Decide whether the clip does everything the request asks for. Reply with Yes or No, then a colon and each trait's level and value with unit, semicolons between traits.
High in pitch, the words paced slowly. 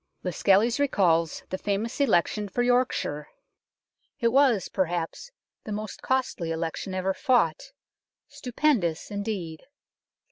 Yes: high, 205 Hz; slow, 110 wpm